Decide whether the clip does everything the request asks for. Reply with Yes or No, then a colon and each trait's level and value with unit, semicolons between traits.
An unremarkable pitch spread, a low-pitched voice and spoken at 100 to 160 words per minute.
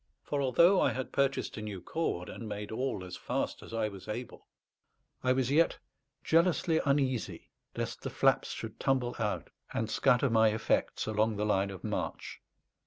No: average, 4.5 semitones; low, 120 Hz; average, 175 wpm